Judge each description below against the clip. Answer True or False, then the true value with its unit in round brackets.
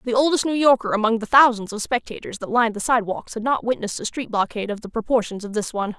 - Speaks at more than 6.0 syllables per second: True (7.0 syllables/s)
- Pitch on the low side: False (230 Hz)